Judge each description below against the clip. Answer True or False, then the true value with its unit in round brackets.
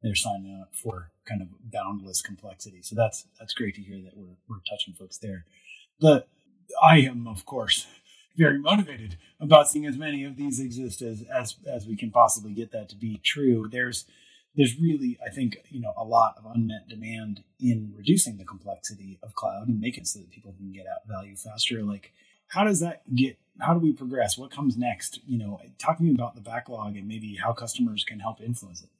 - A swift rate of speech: True (210 wpm)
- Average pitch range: True (4.1 semitones)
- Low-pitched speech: True (115 Hz)